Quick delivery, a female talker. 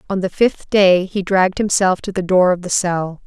Yes: fast, 240 wpm; female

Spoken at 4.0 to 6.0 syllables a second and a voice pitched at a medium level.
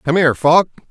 No: 6.6 syllables/s; medium, 155 Hz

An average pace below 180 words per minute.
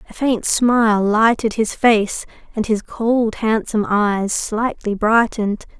Yes: slow, 135 wpm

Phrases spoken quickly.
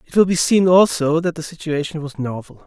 Yes: fast, 225 wpm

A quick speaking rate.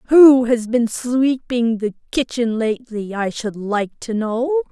No: average, 155 wpm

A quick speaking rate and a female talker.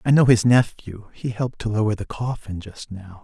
No: fast, 220 wpm; male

